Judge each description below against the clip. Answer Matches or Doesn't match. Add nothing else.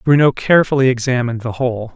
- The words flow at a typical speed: Matches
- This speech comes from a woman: Doesn't match